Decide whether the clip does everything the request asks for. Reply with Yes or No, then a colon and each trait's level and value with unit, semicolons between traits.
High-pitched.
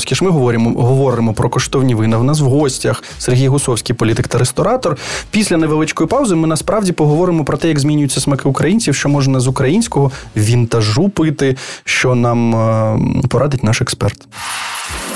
No: low, 135 Hz